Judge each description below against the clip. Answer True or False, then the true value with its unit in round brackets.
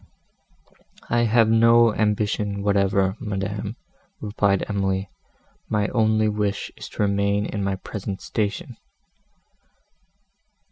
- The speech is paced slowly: True (100 wpm)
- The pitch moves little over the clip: True (1.6 semitones)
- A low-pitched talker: True (105 Hz)